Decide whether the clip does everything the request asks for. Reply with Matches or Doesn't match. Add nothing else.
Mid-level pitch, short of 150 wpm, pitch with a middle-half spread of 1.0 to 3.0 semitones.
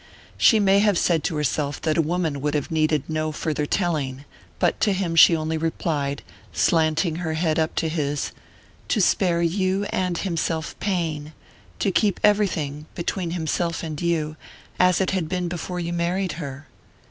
Doesn't match